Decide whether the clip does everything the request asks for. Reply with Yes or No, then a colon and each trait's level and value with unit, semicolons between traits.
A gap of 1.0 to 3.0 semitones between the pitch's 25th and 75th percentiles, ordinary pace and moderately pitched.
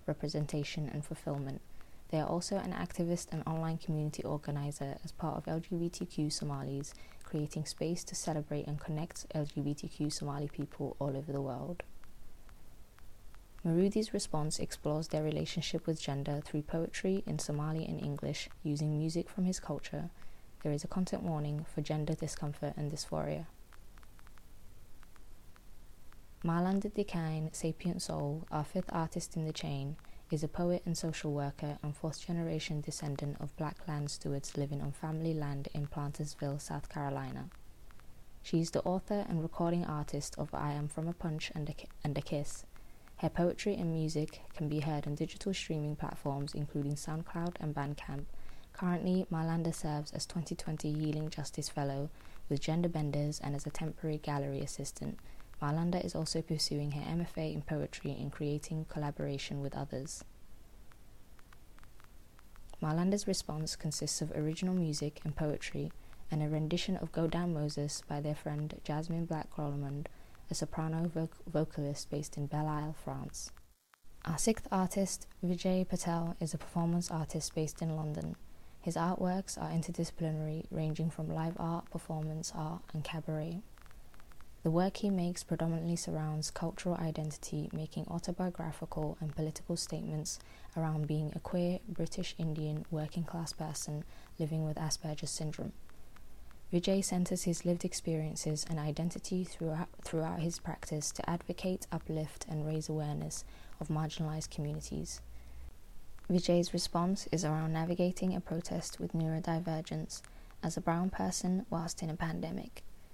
Yes: narrow, 2.4 semitones; average, 145 wpm; medium, 155 Hz